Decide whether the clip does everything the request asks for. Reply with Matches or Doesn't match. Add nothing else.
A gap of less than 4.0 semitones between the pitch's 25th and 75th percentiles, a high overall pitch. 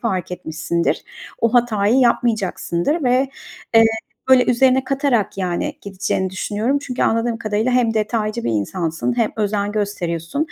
Doesn't match